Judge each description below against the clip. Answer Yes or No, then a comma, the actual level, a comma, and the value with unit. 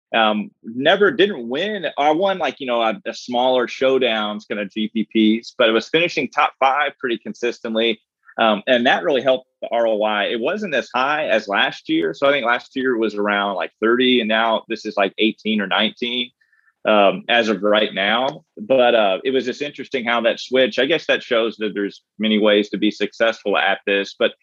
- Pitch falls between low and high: No, low, 115 Hz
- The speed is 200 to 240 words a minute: Yes, fast, 205 wpm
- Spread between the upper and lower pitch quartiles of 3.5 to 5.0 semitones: No, average, 3.0 semitones